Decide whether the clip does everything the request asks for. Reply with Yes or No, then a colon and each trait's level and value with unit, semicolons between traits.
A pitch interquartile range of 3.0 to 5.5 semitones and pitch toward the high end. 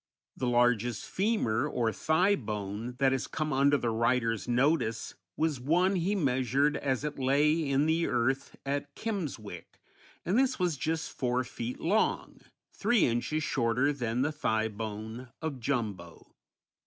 No: average, 4.8 semitones; low, 135 Hz